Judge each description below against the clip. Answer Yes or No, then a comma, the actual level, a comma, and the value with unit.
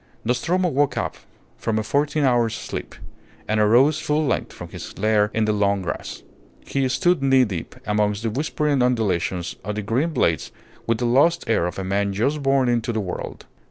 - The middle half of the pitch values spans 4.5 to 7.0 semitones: Yes, average, 4.9 semitones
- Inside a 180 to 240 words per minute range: Yes, average, 190 wpm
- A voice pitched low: Yes, low, 115 Hz